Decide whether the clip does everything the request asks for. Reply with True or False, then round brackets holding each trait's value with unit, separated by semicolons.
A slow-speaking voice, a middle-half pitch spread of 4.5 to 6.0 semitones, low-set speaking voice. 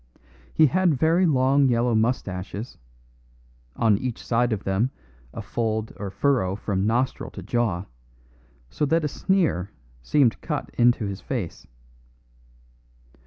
True (125 wpm; 5.1 semitones; 120 Hz)